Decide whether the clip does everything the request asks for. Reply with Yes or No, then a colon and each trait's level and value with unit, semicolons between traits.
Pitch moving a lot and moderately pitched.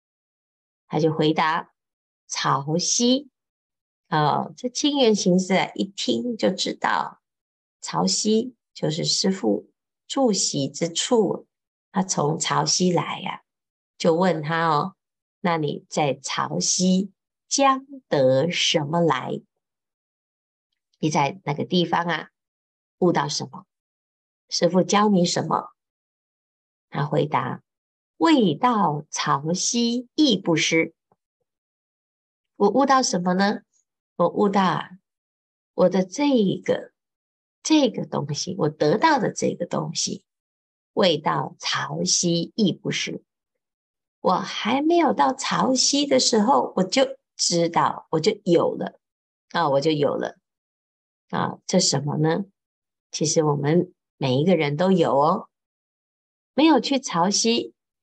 Yes: wide, 6.5 semitones; medium, 180 Hz